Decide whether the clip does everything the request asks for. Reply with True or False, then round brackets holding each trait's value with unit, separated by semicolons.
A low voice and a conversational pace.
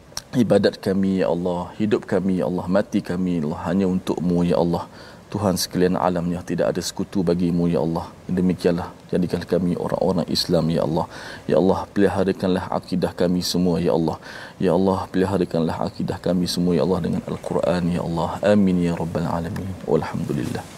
False (90 Hz; 165 wpm)